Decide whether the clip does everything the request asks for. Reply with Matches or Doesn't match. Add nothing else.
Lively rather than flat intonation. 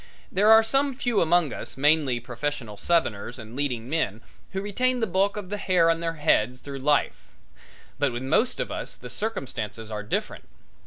Matches